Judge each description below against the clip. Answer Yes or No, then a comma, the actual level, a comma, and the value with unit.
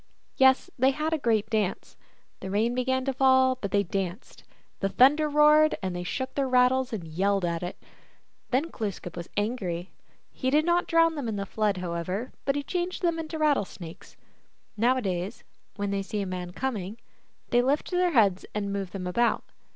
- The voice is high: Yes, high, 230 Hz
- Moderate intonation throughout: No, wide, 5.8 semitones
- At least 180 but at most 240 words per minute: Yes, average, 185 wpm